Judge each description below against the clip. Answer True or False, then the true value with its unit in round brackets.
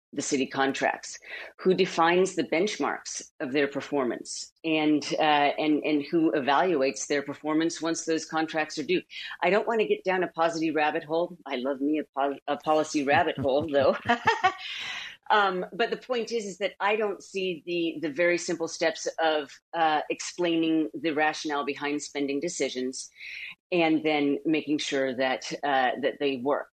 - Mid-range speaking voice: True (160 Hz)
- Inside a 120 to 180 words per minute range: True (170 wpm)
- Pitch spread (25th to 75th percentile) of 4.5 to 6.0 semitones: False (3.3 semitones)